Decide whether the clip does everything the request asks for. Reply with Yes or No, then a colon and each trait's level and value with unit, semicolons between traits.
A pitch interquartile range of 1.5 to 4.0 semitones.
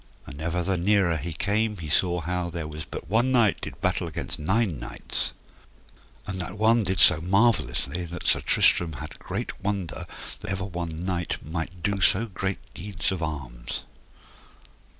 Yes: average, 3.7 semitones